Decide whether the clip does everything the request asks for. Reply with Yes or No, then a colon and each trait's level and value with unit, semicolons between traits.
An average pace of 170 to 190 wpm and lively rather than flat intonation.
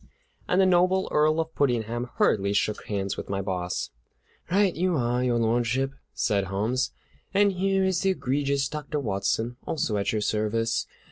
No: average, 160 wpm; wide, 7.4 semitones